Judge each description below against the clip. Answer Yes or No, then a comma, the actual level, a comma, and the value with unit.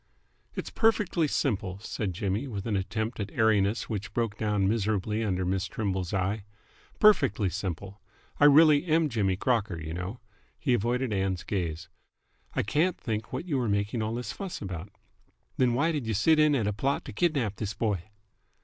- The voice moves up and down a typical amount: Yes, average, 4.8 semitones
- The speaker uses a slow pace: No, average, 175 wpm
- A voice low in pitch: Yes, low, 110 Hz